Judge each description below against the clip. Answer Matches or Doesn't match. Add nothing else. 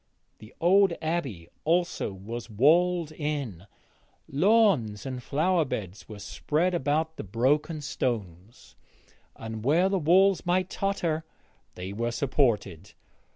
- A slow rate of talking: Matches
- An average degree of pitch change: Doesn't match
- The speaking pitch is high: Doesn't match